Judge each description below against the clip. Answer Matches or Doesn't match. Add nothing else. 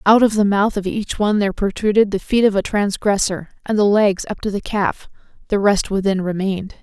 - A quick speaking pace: Matches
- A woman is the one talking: Matches